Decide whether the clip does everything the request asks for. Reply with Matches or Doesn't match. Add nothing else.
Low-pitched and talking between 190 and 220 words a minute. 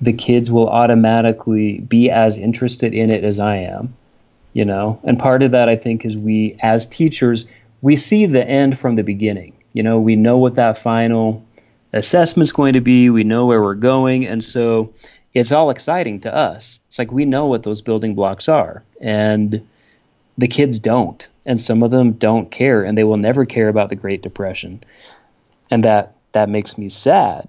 Matches